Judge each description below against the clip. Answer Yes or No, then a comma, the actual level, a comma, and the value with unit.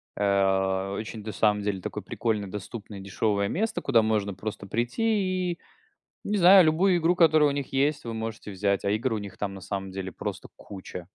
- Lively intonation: Yes, wide, 7.0 semitones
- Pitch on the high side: No, low, 110 Hz